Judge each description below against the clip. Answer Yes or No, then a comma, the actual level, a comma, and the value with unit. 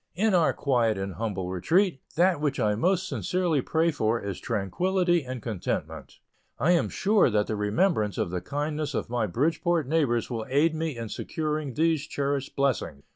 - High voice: No, medium, 140 Hz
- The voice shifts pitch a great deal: Yes, wide, 7.1 semitones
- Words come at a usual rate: Yes, average, 175 wpm